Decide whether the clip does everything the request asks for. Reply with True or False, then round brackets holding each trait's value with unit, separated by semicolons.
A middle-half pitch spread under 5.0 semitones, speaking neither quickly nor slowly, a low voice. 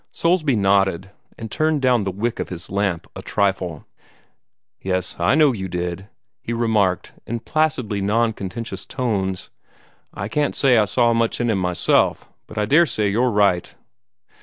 True (4.0 semitones; 160 wpm; 105 Hz)